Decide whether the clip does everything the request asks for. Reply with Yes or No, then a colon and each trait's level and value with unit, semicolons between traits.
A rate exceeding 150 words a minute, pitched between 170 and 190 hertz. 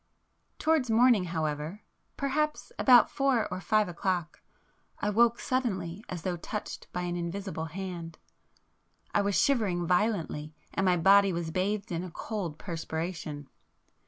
No: slow, 135 wpm; medium, 185 Hz